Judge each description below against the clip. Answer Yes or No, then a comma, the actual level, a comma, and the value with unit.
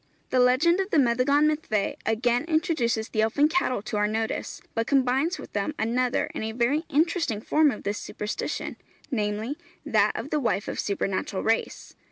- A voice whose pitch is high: Yes, high, 245 Hz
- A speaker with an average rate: Yes, average, 175 wpm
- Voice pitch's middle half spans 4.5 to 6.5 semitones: Yes, wide, 5.5 semitones